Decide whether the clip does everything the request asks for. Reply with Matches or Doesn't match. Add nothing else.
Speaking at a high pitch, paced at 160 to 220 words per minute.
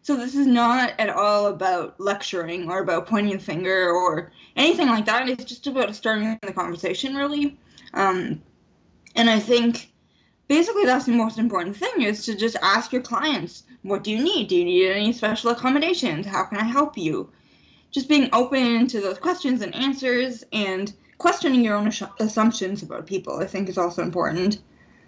Matches